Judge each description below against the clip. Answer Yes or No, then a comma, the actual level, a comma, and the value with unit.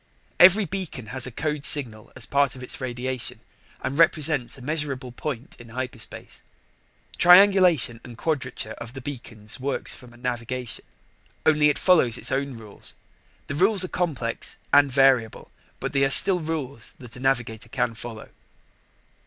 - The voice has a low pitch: Yes, low, 130 Hz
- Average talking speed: Yes, average, 155 wpm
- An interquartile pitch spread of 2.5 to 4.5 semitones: Yes, average, 4.0 semitones